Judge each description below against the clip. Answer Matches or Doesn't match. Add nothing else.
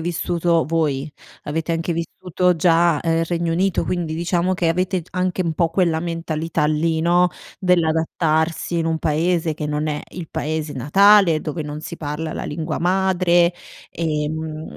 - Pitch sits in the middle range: Matches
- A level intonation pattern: Matches